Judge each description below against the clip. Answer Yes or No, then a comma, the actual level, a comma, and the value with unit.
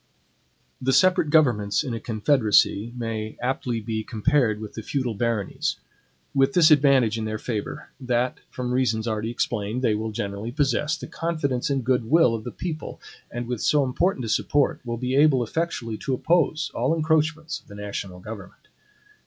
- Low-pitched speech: Yes, low, 125 Hz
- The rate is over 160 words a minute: Yes, average, 175 wpm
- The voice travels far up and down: No, average, 4.7 semitones